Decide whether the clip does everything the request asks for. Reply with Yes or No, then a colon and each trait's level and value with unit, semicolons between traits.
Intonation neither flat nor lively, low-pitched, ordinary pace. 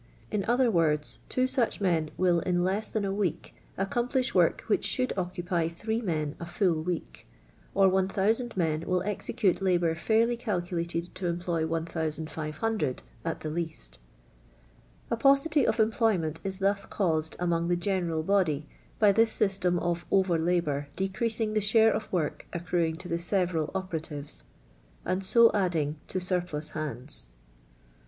No: average, 3.9 semitones; medium, 180 Hz; average, 160 wpm